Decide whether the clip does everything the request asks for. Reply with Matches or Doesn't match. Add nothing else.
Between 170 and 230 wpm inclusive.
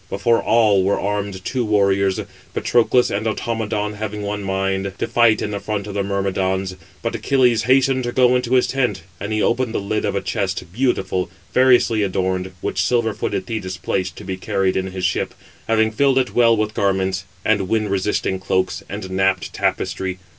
Matches